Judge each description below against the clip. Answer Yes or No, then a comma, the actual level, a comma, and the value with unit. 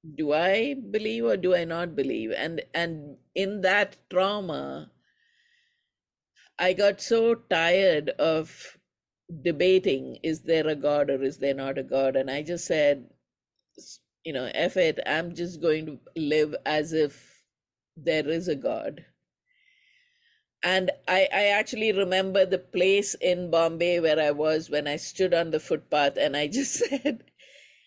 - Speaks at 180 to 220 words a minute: No, average, 150 wpm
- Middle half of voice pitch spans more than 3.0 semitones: Yes, average, 5.1 semitones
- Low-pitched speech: No, medium, 175 Hz